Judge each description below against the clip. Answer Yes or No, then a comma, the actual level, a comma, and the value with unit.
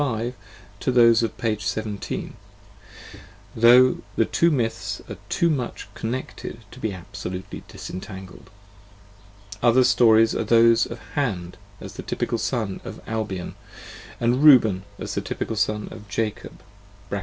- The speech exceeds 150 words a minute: No, average, 140 wpm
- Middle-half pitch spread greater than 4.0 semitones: No, average, 2.9 semitones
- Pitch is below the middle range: Yes, low, 115 Hz